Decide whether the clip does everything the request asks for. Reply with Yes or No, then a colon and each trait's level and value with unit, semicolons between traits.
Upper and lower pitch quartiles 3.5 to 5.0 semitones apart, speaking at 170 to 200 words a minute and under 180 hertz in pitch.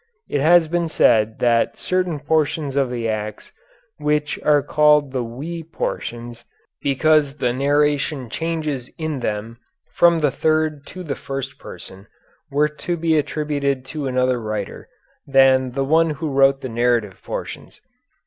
No: average, 3.8 semitones; average, 145 wpm; medium, 140 Hz